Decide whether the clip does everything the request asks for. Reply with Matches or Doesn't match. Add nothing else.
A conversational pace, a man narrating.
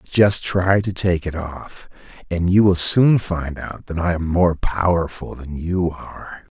Matches